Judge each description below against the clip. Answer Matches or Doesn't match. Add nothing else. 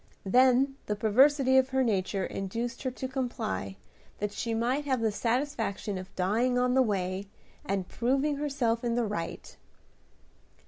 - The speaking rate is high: Doesn't match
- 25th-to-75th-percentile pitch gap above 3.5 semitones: Matches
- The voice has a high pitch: Matches